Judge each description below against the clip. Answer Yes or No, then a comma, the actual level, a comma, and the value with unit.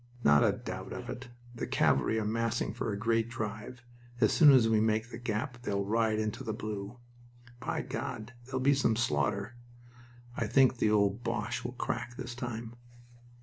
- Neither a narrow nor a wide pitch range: No, narrow, 2.2 semitones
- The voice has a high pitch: No, low, 115 Hz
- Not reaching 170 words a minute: No, average, 180 wpm